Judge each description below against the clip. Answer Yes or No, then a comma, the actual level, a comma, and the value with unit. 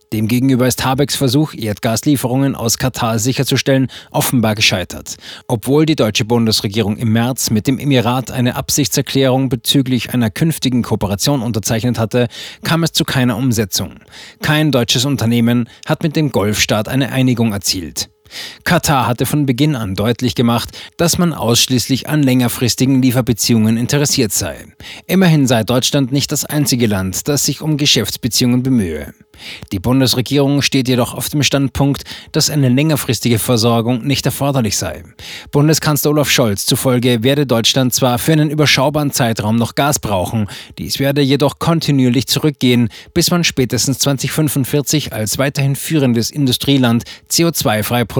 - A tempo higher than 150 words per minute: No, average, 140 wpm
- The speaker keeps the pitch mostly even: No, average, 3.5 semitones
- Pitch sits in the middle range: No, low, 130 Hz